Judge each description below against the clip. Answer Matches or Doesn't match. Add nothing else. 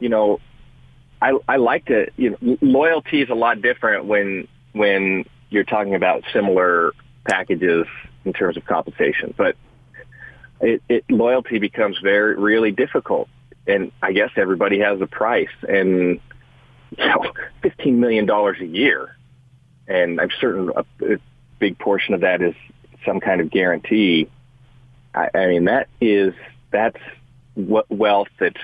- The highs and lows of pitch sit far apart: Doesn't match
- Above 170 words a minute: Doesn't match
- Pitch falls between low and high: Doesn't match